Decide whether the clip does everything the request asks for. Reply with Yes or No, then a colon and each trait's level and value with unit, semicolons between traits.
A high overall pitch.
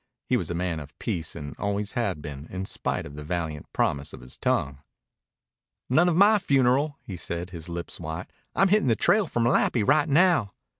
No: very low, 95 Hz